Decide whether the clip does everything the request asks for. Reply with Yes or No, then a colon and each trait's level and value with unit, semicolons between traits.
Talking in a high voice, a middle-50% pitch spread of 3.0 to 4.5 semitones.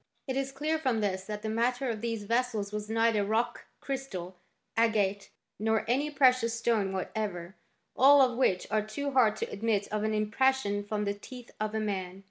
Yes: high, 220 Hz; average, 3.5 semitones